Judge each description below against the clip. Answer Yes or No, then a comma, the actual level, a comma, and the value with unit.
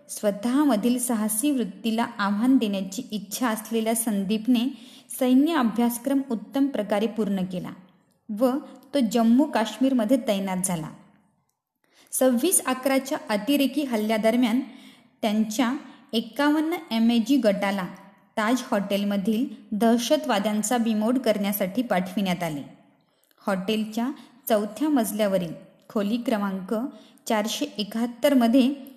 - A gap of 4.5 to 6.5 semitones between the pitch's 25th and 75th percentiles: No, average, 3.6 semitones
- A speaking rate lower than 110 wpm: Yes, average, 90 wpm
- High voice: Yes, high, 230 Hz